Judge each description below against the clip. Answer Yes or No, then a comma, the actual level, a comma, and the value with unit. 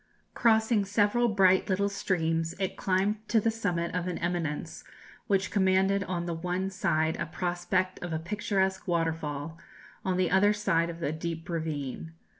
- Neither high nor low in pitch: Yes, medium, 180 Hz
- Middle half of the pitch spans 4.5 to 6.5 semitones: No, average, 3.1 semitones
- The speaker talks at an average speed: Yes, average, 160 wpm